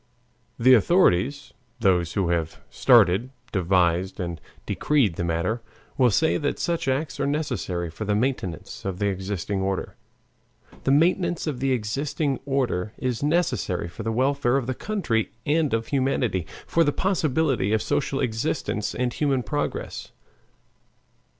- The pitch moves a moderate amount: No, wide, 6.8 semitones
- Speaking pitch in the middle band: No, low, 120 Hz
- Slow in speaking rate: No, average, 145 wpm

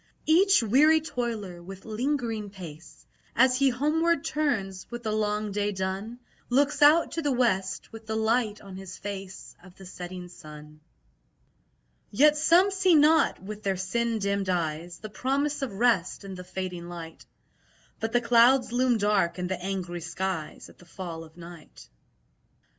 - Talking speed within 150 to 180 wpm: Yes, average, 160 wpm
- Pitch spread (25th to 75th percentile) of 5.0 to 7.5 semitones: Yes, wide, 5.4 semitones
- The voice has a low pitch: No, high, 210 Hz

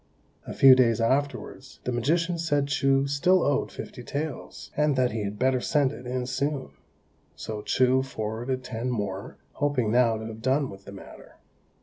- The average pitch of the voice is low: Yes, low, 130 Hz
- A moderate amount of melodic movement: Yes, average, 3.7 semitones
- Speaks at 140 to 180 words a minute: Yes, average, 175 wpm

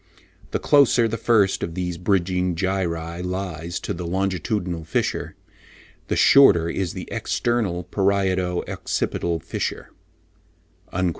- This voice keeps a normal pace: No, slow, 120 wpm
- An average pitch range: No, narrow, 2.3 semitones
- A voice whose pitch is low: Yes, very low, 90 Hz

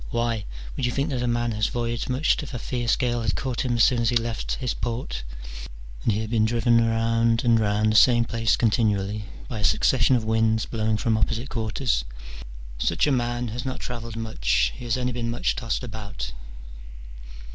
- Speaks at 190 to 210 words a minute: Yes, average, 200 wpm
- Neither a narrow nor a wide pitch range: No, narrow, 1.7 semitones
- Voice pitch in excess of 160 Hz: No, low, 115 Hz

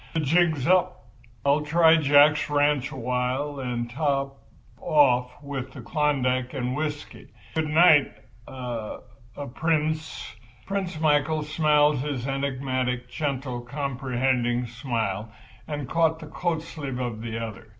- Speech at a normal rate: No, slow, 115 wpm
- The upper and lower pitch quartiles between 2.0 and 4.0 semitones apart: Yes, average, 3.4 semitones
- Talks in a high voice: No, medium, 140 Hz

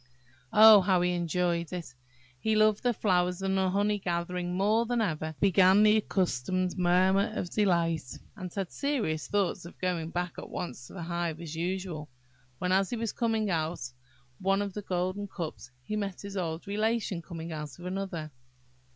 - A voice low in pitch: No, medium, 185 Hz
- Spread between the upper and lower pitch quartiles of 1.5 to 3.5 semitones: Yes, average, 3.0 semitones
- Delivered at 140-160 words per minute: No, average, 185 wpm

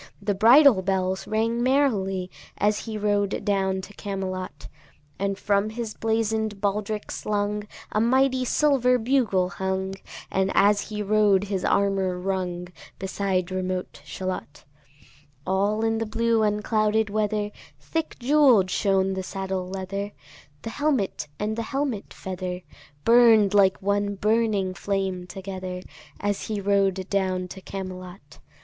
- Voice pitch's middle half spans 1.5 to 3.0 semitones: Yes, narrow, 2.5 semitones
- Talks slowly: Yes, slow, 130 wpm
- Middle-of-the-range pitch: No, high, 200 Hz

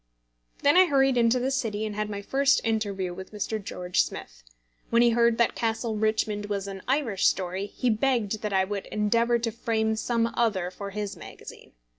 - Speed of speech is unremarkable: Yes, average, 190 wpm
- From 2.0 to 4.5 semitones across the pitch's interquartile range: Yes, average, 2.7 semitones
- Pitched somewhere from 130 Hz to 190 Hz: No, high, 220 Hz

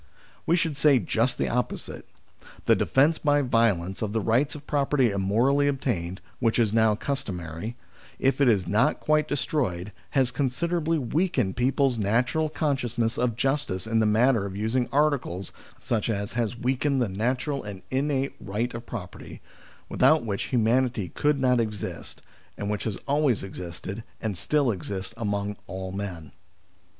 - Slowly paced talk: No, average, 155 wpm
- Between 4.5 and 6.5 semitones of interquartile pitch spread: Yes, average, 5.2 semitones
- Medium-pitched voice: No, low, 120 Hz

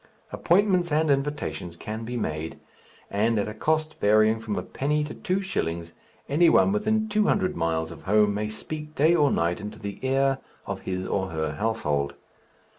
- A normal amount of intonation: No, wide, 8.6 semitones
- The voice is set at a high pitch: No, low, 115 Hz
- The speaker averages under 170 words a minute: No, average, 180 wpm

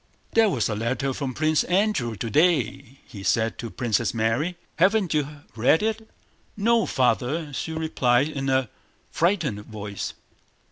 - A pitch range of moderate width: No, wide, 6.4 semitones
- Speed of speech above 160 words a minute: No, slow, 135 wpm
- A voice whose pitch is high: No, low, 135 Hz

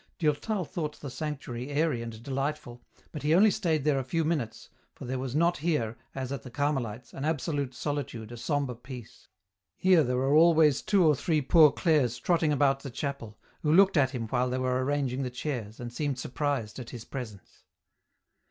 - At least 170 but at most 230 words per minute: Yes, average, 190 wpm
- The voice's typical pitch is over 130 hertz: Yes, medium, 140 Hz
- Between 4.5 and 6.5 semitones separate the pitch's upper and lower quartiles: No, average, 3.7 semitones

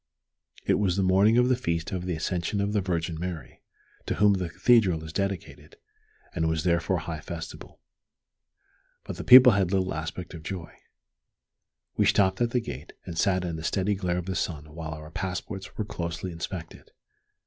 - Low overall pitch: Yes, very low, 90 Hz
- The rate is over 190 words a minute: No, average, 180 wpm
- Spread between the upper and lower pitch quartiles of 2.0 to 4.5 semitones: Yes, average, 3.0 semitones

